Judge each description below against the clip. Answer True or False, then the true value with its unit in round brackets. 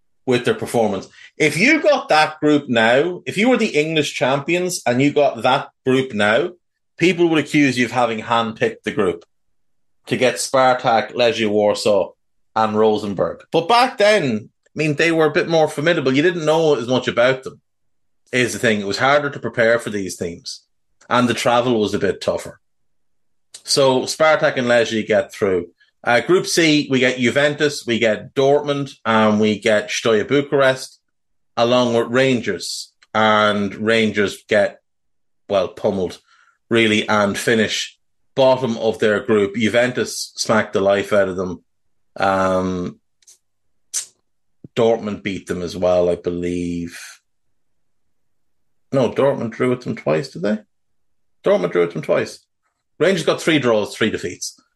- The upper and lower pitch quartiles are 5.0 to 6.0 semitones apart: True (5.6 semitones)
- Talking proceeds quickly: False (155 wpm)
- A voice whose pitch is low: True (120 Hz)